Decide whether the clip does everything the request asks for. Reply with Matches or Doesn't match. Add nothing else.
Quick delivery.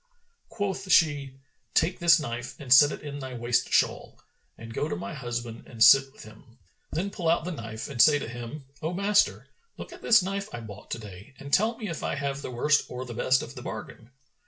Matches